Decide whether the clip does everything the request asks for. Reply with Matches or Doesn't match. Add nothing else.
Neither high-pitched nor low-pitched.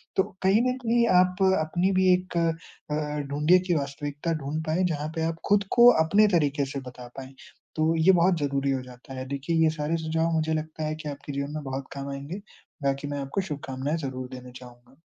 Matches